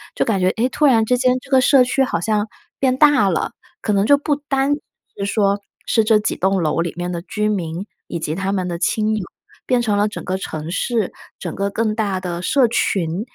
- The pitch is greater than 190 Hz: Yes, high, 210 Hz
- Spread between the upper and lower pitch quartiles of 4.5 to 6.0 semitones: Yes, average, 5.1 semitones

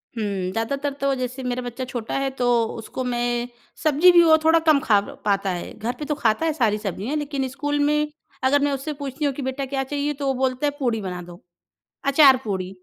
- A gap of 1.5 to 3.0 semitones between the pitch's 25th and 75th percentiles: No, average, 4.3 semitones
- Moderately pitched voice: No, very high, 265 Hz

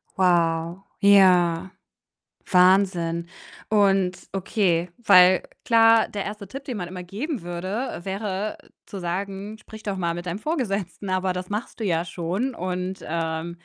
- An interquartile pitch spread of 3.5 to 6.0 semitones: No, average, 2.8 semitones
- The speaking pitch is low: No, medium, 185 Hz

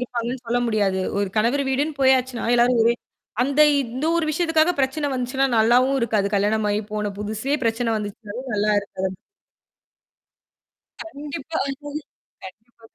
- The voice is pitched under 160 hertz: No, high, 240 Hz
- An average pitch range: Yes, average, 4.2 semitones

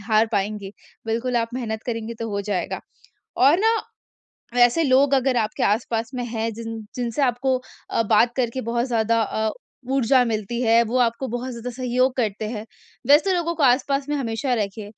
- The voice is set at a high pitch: Yes, high, 235 Hz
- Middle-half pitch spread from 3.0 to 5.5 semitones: No, narrow, 2.6 semitones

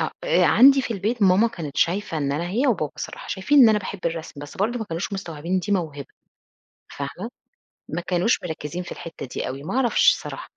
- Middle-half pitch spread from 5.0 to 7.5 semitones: Yes, wide, 5.6 semitones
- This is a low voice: No, medium, 185 Hz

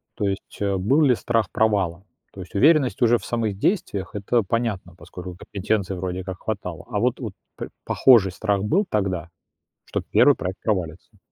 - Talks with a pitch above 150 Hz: No, low, 100 Hz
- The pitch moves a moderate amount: Yes, average, 3.8 semitones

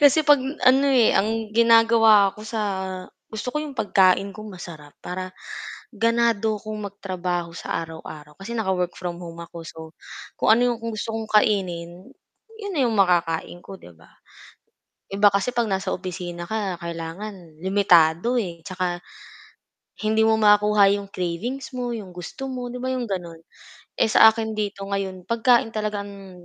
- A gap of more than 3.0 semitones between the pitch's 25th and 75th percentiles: Yes, average, 4.0 semitones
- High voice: Yes, high, 200 Hz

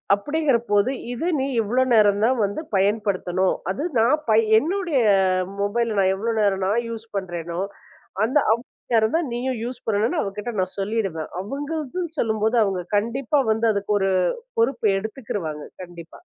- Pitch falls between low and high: No, high, 220 Hz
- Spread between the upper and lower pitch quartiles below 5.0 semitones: Yes, average, 4.2 semitones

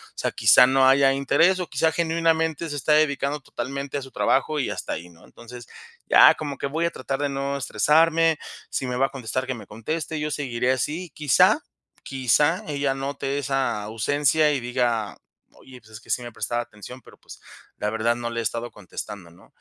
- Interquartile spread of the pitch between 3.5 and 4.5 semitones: Yes, average, 3.8 semitones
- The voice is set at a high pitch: No, low, 135 Hz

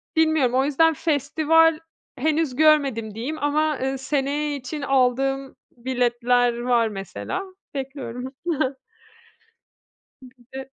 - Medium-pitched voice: No, very high, 270 Hz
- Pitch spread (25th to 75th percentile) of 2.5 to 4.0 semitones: Yes, average, 3.3 semitones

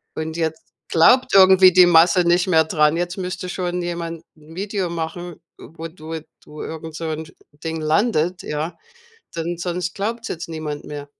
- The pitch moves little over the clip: Yes, narrow, 2.2 semitones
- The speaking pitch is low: No, medium, 170 Hz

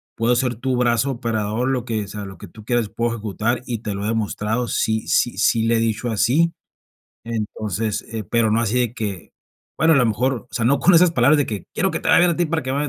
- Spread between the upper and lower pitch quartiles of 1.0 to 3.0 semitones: Yes, average, 2.7 semitones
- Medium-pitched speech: No, low, 115 Hz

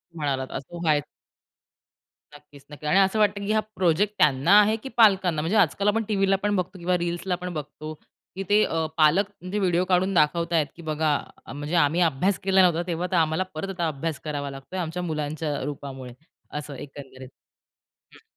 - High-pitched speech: No, medium, 170 Hz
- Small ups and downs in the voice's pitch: No, average, 4.3 semitones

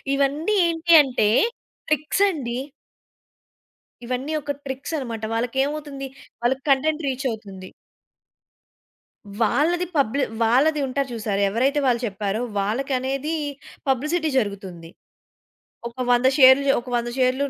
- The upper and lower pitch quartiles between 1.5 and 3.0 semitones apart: No, average, 3.7 semitones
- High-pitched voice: Yes, very high, 265 Hz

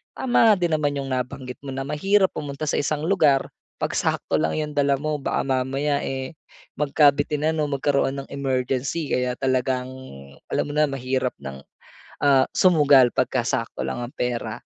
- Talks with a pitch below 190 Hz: Yes, medium, 140 Hz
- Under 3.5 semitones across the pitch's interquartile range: Yes, narrow, 2.5 semitones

